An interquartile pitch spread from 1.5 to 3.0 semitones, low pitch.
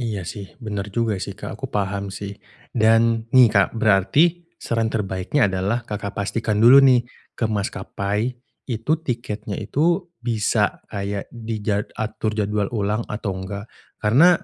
Yes: average, 2.7 semitones; low, 110 Hz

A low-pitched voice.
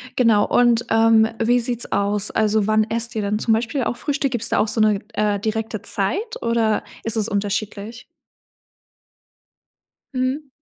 No: high, 225 Hz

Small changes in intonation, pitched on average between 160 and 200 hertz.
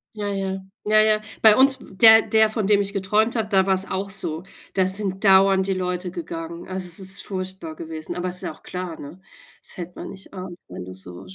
Yes: narrow, 2.2 semitones; high, 190 Hz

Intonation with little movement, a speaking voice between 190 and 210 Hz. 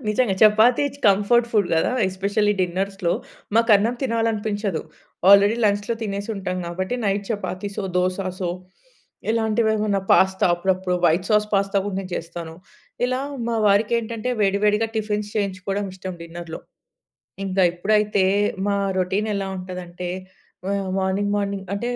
Yes: narrow, 2.2 semitones; high, 200 Hz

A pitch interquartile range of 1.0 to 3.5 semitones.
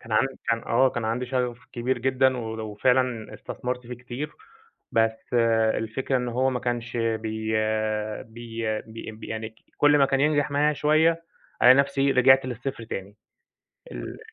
Yes: average, 2.9 semitones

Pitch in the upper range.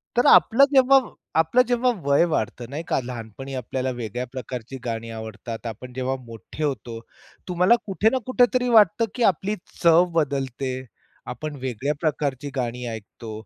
No: low, 135 Hz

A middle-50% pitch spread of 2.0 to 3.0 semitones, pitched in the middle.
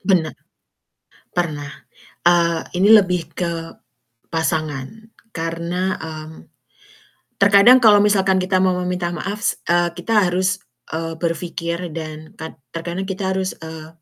Yes: narrow, 2.6 semitones; medium, 175 Hz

